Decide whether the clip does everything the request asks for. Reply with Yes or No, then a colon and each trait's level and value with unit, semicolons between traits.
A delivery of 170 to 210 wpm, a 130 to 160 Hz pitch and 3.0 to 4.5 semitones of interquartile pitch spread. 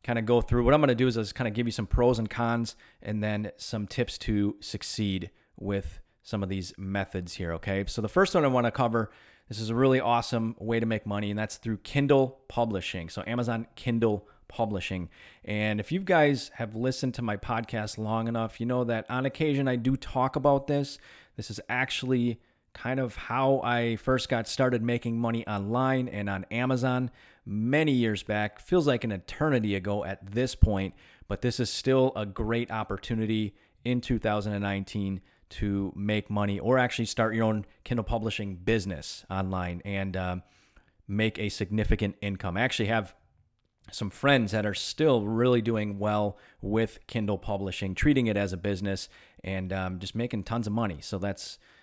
No: average, 185 wpm; low, 110 Hz; average, 3.4 semitones